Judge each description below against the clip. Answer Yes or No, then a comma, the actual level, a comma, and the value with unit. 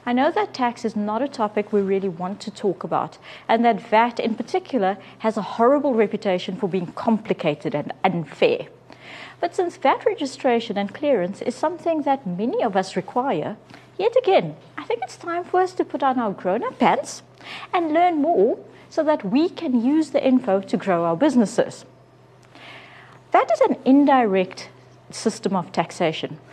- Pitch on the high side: Yes, high, 235 Hz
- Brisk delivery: No, average, 175 wpm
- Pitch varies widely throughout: Yes, wide, 7.8 semitones